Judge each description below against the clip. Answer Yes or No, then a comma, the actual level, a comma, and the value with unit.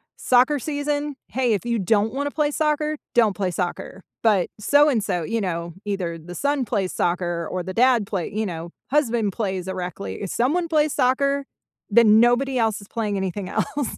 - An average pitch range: No, wide, 6.7 semitones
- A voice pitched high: Yes, high, 225 Hz